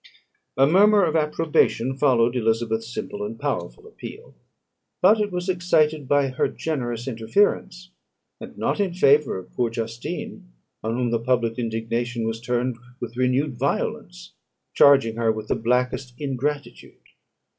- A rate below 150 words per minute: Yes, average, 140 wpm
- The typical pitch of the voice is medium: No, low, 130 Hz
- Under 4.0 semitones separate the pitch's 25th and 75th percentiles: No, average, 5.3 semitones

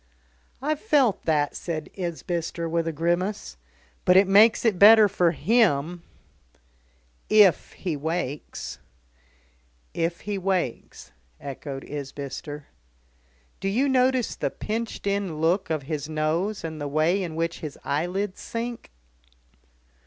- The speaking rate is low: Yes, slow, 125 wpm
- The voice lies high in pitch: No, medium, 175 Hz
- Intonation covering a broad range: No, average, 4.7 semitones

